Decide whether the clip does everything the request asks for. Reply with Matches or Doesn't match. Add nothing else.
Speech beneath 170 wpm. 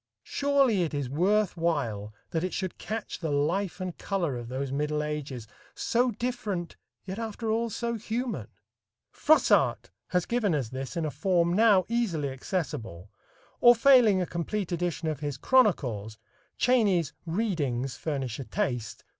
Matches